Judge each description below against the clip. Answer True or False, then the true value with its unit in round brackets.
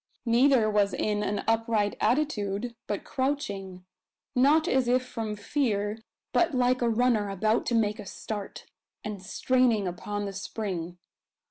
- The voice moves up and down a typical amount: True (3.6 semitones)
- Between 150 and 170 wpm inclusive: False (140 wpm)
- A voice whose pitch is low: False (220 Hz)